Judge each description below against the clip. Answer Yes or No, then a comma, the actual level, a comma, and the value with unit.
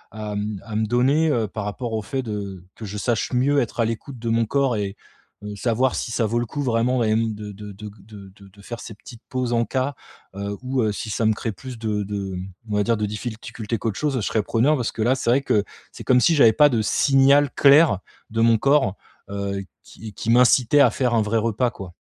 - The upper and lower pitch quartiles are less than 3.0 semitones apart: No, average, 3.3 semitones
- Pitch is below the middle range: Yes, low, 115 Hz